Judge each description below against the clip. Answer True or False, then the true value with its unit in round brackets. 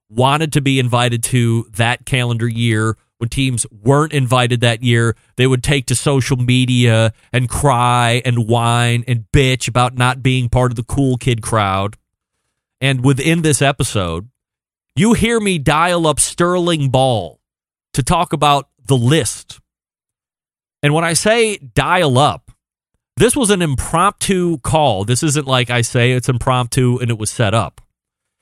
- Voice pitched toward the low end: True (125 Hz)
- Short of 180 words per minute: True (155 wpm)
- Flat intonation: False (3.5 semitones)